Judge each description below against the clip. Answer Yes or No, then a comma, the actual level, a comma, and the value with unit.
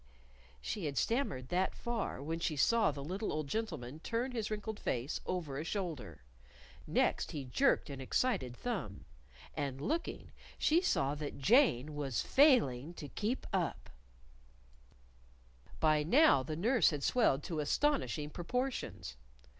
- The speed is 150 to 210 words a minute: No, average, 140 wpm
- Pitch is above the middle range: No, medium, 165 Hz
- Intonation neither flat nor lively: No, wide, 8.6 semitones